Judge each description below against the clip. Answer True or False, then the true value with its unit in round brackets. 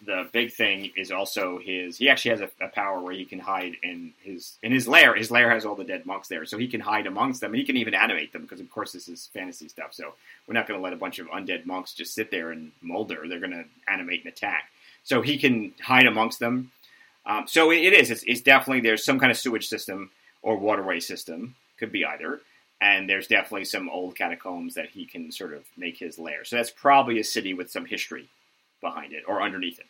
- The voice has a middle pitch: False (115 Hz)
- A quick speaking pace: True (245 wpm)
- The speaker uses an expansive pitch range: True (6.5 semitones)